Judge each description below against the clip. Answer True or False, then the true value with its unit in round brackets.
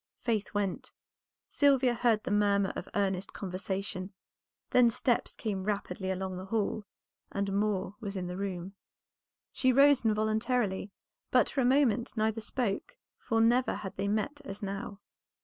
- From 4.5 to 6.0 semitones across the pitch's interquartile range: False (3.2 semitones)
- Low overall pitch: False (205 Hz)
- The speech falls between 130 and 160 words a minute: True (150 wpm)